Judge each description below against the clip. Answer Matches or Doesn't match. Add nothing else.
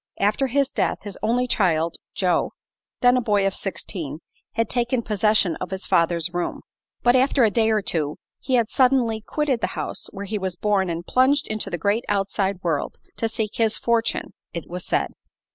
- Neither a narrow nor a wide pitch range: Matches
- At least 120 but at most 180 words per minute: Doesn't match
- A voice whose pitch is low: Doesn't match